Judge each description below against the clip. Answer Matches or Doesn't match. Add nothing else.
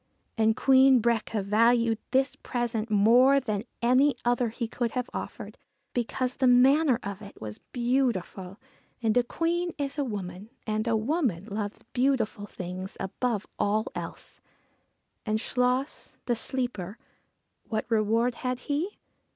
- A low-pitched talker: Doesn't match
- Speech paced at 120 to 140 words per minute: Matches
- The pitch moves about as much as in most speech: Matches